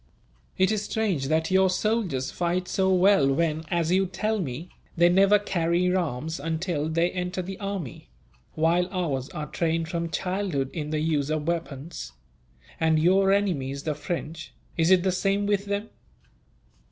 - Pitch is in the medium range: Yes, medium, 170 Hz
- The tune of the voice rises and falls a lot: No, average, 3.4 semitones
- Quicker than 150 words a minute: Yes, average, 160 wpm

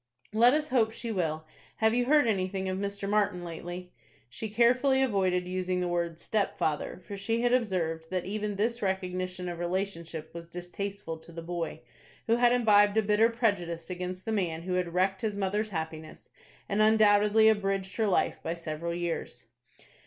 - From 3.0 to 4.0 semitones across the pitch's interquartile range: Yes, average, 3.7 semitones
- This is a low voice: No, high, 190 Hz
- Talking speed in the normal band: Yes, average, 175 wpm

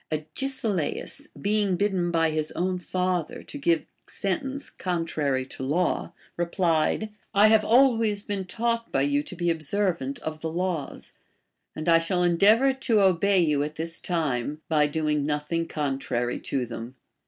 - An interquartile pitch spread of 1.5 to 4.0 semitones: No, average, 4.9 semitones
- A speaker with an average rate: Yes, average, 150 wpm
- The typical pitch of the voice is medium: Yes, medium, 170 Hz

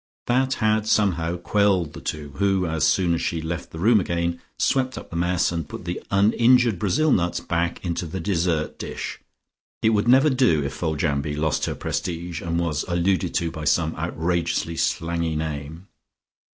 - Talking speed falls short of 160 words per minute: No, average, 175 wpm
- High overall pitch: No, very low, 85 Hz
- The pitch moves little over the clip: No, average, 3.7 semitones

